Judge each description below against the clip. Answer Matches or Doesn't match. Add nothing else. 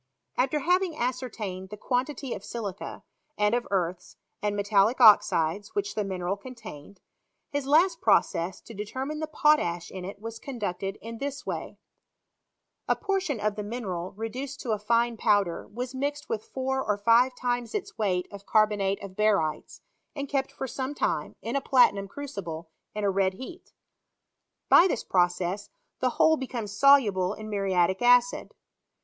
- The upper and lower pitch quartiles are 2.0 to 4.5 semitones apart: Doesn't match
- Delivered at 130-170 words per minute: Matches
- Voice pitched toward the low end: Doesn't match